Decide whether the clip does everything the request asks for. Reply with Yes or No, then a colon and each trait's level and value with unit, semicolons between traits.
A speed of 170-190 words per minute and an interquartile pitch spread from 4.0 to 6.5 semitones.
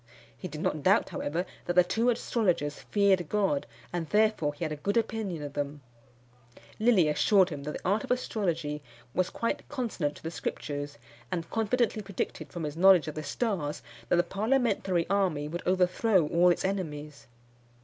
Yes: average, 175 wpm; average, 5.3 semitones